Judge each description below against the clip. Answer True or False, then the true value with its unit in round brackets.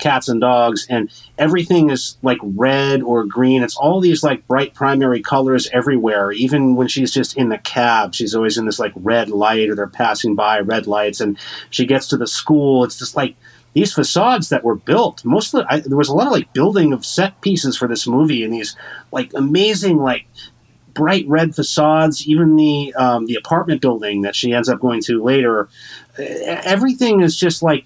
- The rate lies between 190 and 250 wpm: True (200 wpm)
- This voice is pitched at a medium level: False (130 Hz)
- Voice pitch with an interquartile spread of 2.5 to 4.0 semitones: False (4.5 semitones)